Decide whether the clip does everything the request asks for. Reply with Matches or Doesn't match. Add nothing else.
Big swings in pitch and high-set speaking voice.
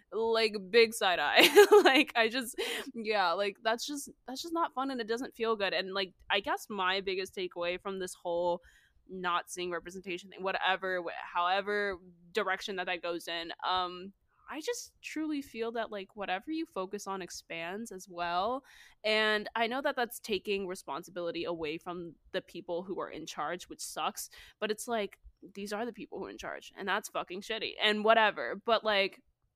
Doesn't match